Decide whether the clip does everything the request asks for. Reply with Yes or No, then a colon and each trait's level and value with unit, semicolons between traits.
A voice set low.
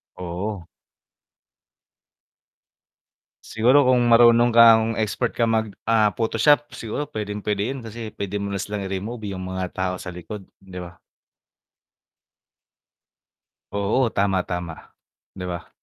Yes: low, 105 Hz